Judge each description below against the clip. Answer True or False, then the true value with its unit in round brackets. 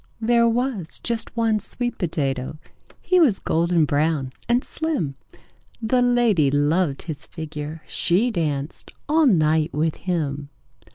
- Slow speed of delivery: True (125 wpm)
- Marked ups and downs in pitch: True (7.5 semitones)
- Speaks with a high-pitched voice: False (170 Hz)